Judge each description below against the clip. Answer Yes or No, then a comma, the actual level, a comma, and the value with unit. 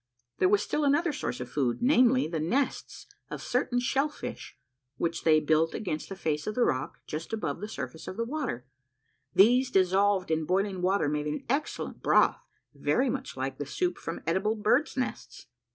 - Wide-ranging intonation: Yes, wide, 7.8 semitones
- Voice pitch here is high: Yes, high, 195 Hz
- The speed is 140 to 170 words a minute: No, average, 185 wpm